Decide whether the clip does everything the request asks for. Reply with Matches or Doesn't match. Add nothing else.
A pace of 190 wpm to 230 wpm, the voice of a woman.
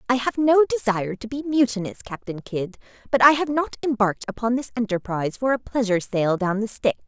Matches